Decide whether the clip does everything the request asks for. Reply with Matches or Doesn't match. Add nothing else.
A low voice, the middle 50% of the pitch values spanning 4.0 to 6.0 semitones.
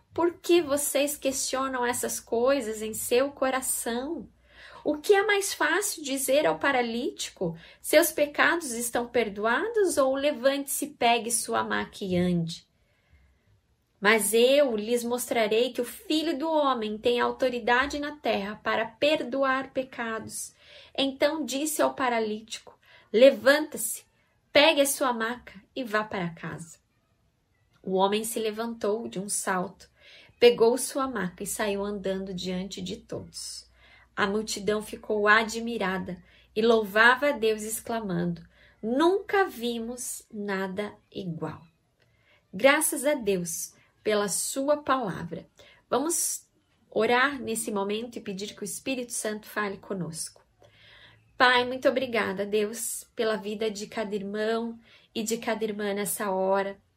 Doesn't match